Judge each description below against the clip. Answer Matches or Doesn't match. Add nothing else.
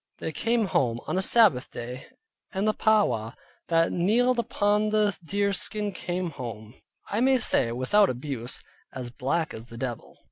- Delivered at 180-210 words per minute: Doesn't match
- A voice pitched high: Doesn't match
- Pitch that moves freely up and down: Matches